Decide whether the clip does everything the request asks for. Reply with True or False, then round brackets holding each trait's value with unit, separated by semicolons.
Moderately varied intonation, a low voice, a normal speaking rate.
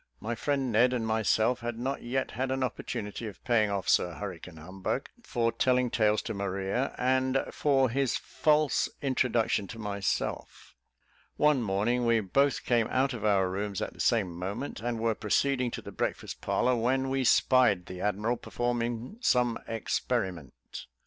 True (3.8 semitones; 115 Hz; 160 wpm)